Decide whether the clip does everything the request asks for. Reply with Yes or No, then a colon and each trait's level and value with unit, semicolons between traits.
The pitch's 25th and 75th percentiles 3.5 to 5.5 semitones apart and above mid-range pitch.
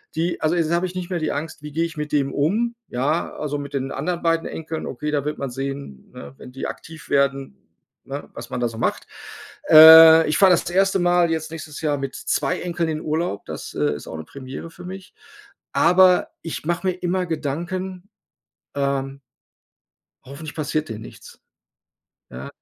No: average, 3.8 semitones; medium, 155 Hz